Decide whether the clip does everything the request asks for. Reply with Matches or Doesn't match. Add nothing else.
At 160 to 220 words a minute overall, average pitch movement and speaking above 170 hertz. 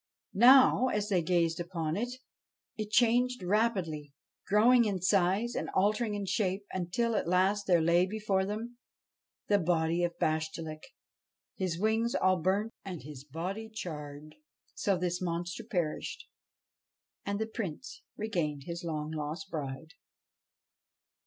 Doesn't match